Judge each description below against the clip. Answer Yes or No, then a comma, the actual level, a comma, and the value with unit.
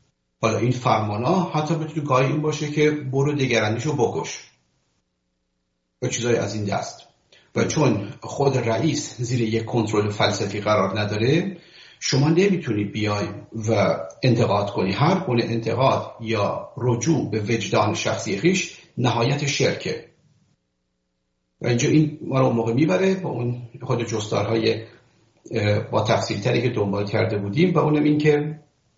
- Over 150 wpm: No, average, 140 wpm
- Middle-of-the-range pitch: No, low, 120 Hz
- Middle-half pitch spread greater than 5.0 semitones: Yes, wide, 5.6 semitones